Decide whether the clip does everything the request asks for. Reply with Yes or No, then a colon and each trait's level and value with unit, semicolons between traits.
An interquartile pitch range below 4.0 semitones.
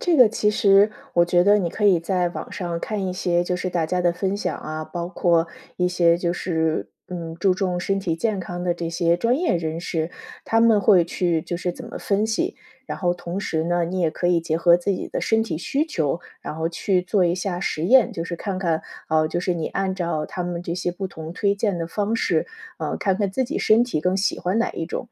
Yes: average, 2.7 semitones